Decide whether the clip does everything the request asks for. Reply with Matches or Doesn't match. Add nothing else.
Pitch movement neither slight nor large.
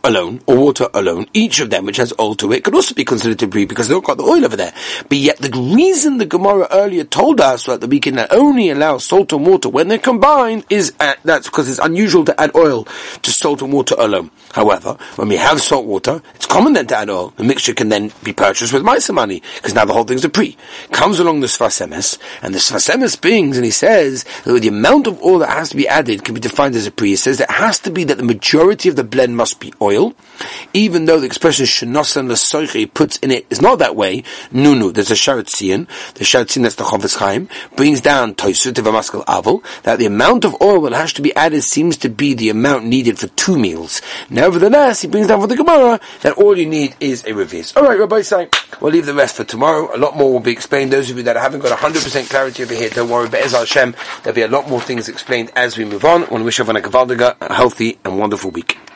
Doesn't match